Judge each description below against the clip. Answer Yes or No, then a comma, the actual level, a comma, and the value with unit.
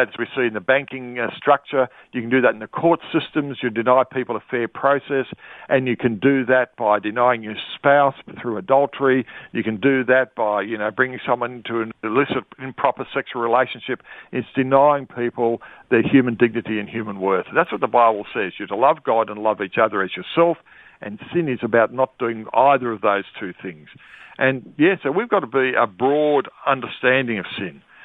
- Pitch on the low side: Yes, low, 125 Hz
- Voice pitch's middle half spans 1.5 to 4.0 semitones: Yes, average, 2.8 semitones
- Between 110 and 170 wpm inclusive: No, fast, 205 wpm